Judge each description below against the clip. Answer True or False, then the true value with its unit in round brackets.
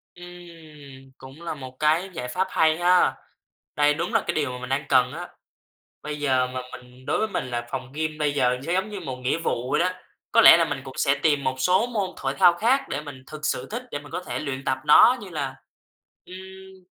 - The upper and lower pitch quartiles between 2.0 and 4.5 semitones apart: False (5.2 semitones)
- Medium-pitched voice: True (150 Hz)